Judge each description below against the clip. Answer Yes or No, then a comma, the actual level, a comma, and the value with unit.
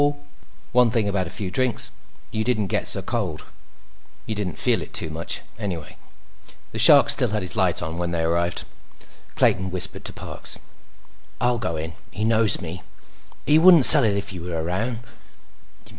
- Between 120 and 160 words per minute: No, average, 175 wpm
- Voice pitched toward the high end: No, low, 100 Hz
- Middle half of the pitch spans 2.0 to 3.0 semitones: No, average, 4.7 semitones